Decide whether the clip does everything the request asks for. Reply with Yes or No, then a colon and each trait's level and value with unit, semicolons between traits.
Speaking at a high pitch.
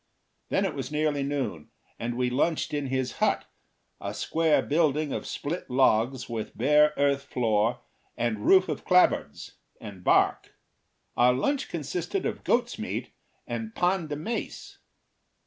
No: medium, 140 Hz